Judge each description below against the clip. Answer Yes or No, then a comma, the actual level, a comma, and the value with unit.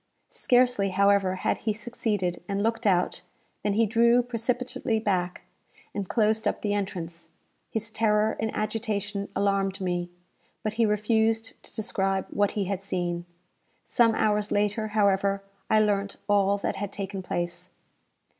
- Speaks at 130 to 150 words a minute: Yes, average, 145 wpm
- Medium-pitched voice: No, high, 205 Hz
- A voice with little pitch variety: Yes, narrow, 2.2 semitones